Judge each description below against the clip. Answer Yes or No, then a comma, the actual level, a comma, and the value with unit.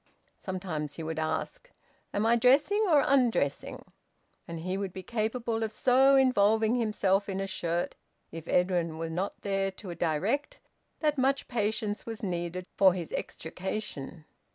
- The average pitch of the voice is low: No, high, 195 Hz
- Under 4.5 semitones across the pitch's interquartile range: No, average, 5.2 semitones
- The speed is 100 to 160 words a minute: Yes, average, 150 wpm